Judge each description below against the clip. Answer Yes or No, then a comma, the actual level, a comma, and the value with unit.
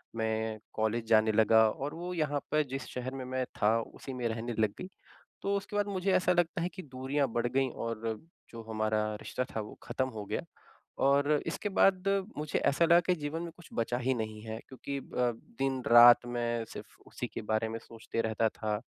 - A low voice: Yes, low, 120 Hz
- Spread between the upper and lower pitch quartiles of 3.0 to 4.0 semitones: No, average, 4.8 semitones